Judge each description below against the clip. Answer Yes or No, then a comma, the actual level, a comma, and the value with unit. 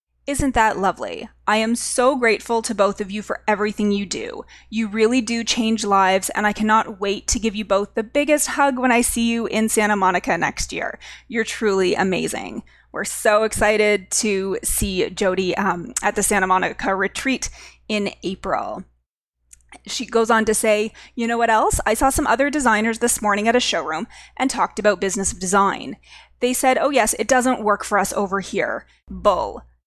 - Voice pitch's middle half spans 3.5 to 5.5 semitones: No, average, 2.8 semitones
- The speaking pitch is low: No, high, 215 Hz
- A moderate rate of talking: Yes, average, 185 wpm